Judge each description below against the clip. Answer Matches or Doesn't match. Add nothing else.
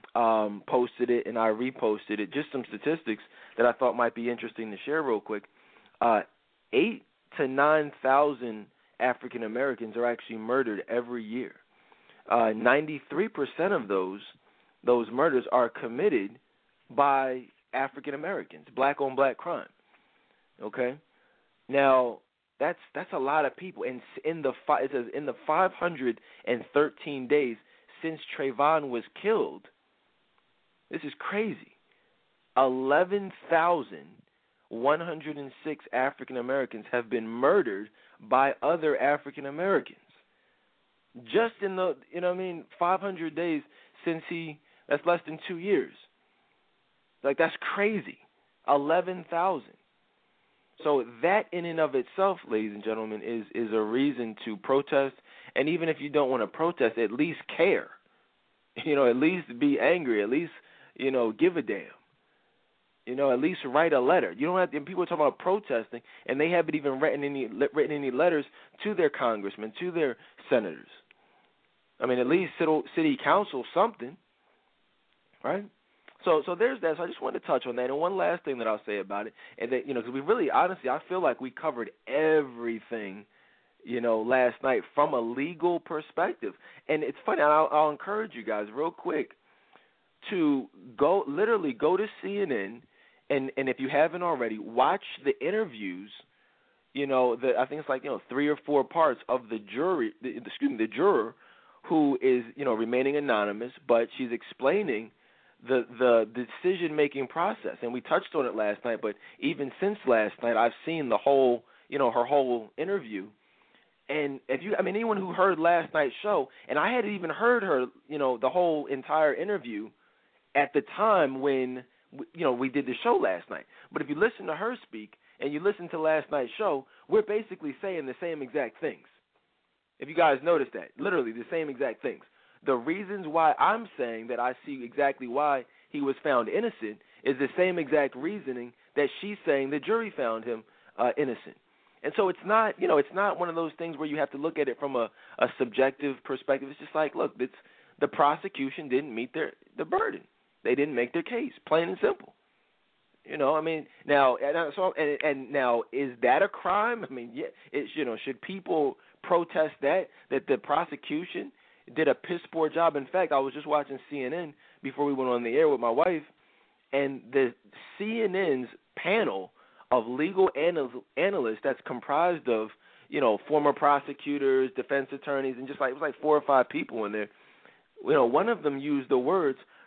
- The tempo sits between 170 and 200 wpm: Matches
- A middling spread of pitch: Doesn't match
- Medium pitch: Matches